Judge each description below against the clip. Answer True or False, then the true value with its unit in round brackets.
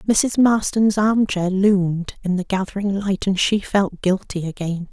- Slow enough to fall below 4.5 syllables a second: True (4.3 syllables/s)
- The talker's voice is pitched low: False (195 Hz)